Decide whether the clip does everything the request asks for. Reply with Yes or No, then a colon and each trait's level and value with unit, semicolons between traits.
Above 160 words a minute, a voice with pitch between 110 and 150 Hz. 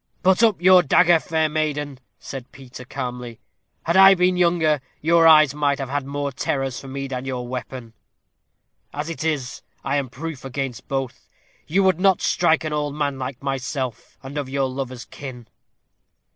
Yes: average, 170 wpm; medium, 140 Hz